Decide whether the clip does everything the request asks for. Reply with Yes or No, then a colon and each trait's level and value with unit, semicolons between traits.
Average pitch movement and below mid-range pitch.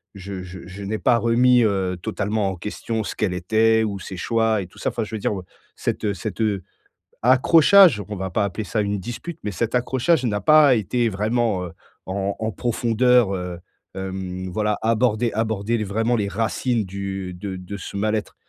Yes: average, 3.2 semitones; low, 105 Hz